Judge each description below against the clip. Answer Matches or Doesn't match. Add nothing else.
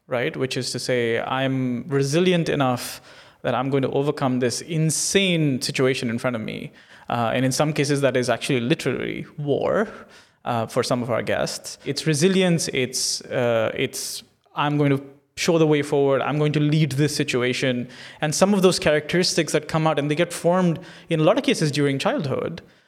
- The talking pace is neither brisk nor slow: Matches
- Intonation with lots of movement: Doesn't match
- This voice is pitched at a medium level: Matches